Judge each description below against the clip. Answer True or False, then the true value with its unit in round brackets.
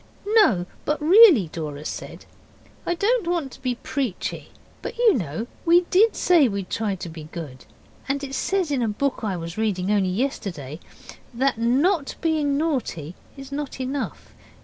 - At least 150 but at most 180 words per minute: True (165 wpm)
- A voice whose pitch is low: False (260 Hz)